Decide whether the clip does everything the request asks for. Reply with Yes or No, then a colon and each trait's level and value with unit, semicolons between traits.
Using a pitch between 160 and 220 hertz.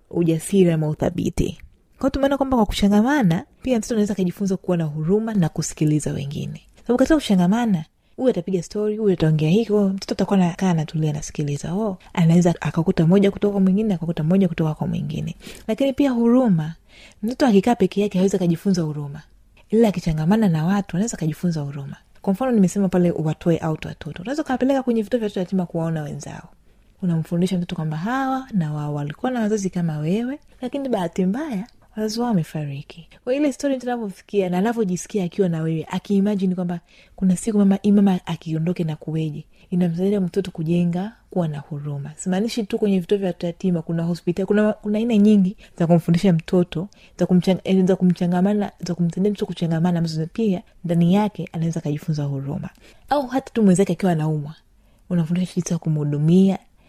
Yes: medium, 185 Hz